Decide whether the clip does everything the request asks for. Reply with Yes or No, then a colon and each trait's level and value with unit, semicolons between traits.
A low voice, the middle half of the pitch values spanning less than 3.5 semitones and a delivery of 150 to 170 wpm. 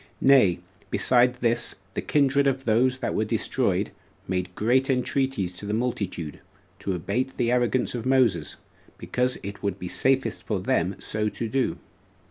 No: low, 120 Hz; average, 4.5 semitones; average, 155 wpm